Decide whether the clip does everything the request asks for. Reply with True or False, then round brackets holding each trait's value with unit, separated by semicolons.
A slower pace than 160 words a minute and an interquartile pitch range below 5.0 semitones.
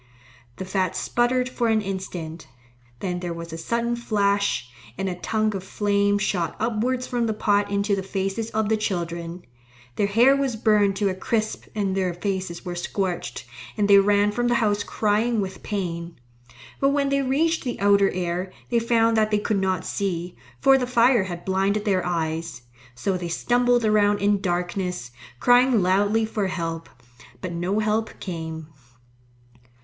False (170 wpm; 3.5 semitones)